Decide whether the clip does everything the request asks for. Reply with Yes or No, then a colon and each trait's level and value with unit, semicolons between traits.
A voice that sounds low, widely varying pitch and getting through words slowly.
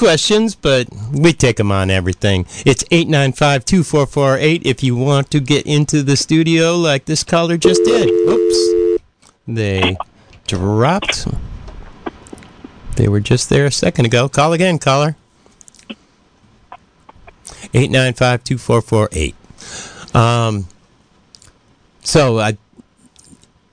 Yes: low, 125 Hz; wide, 5.7 semitones; slow, 100 wpm